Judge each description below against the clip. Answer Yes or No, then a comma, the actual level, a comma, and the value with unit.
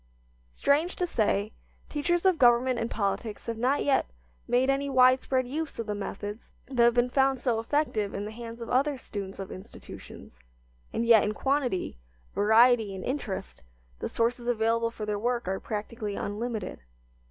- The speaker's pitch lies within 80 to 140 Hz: No, high, 235 Hz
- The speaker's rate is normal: Yes, average, 165 wpm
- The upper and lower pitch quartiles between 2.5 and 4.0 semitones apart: Yes, average, 3.7 semitones